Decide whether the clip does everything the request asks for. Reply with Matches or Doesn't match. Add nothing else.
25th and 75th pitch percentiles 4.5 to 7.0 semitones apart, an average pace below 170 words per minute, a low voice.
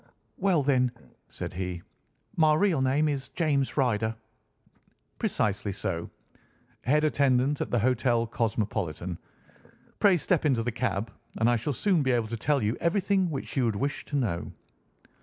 Matches